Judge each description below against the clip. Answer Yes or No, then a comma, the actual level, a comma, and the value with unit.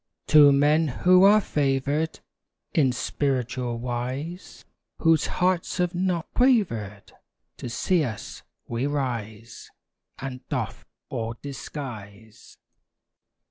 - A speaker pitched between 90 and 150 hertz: Yes, medium, 140 Hz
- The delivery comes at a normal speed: No, slow, 100 wpm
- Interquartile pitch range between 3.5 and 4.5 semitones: No, average, 5.3 semitones